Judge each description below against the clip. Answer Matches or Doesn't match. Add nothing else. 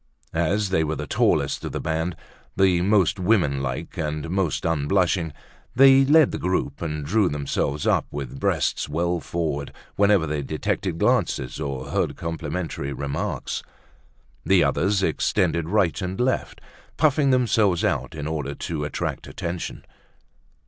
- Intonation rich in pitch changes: Doesn't match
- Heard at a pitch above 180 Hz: Doesn't match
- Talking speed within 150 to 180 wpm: Doesn't match